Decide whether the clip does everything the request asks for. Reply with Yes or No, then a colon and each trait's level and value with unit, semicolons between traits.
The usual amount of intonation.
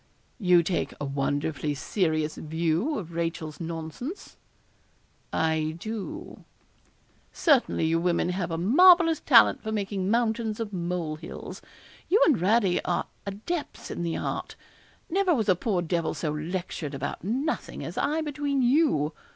No: wide, 7.1 semitones